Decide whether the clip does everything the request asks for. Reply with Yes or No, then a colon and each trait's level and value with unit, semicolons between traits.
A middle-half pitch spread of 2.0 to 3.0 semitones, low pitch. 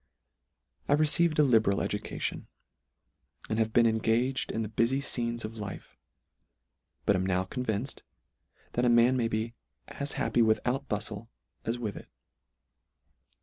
Yes: narrow, 2.6 semitones; low, 115 Hz